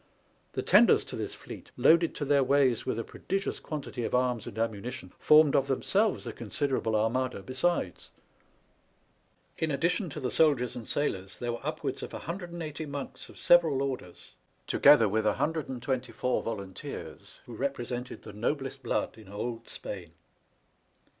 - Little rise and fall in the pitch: No, average, 4.5 semitones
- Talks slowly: No, average, 150 wpm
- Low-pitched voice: Yes, low, 130 Hz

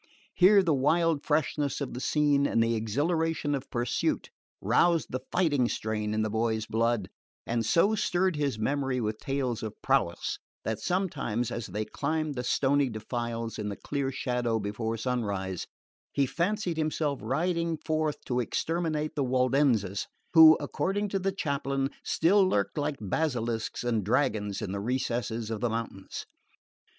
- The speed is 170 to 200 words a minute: No, average, 155 wpm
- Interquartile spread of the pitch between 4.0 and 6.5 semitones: Yes, wide, 5.6 semitones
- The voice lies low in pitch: Yes, low, 130 Hz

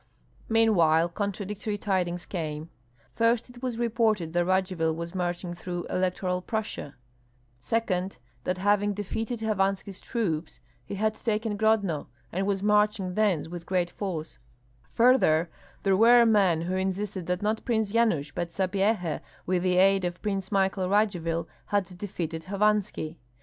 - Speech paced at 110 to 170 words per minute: Yes, average, 140 wpm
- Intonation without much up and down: No, average, 3.3 semitones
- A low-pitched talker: No, high, 190 Hz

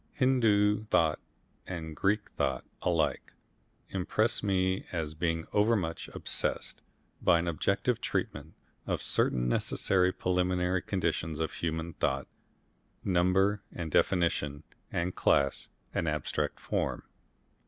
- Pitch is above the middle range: No, very low, 90 Hz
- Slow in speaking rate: Yes, slow, 110 wpm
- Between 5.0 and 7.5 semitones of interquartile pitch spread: No, average, 3.3 semitones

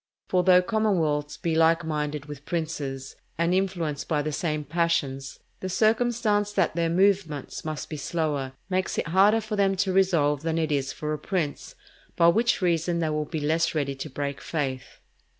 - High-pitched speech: No, medium, 165 Hz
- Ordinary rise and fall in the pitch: Yes, average, 4.0 semitones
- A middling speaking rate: Yes, average, 180 wpm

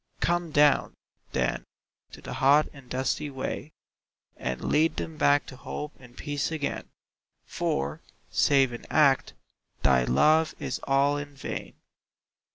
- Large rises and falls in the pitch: No, narrow, 2.5 semitones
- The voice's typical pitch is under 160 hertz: Yes, medium, 140 Hz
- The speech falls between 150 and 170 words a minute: No, slow, 135 wpm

